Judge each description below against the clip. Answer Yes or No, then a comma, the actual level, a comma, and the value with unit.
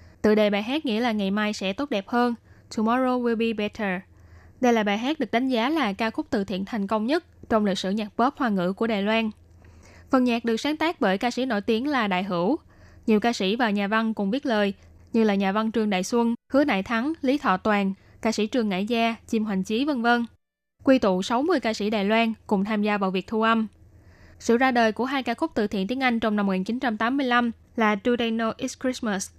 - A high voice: Yes, high, 225 Hz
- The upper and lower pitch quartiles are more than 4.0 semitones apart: No, average, 3.1 semitones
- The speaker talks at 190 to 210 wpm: No, average, 245 wpm